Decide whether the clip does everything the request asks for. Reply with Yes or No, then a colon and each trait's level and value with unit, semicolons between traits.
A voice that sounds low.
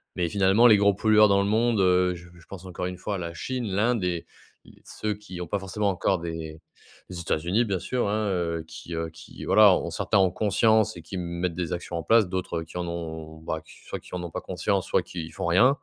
Yes: very low, 90 Hz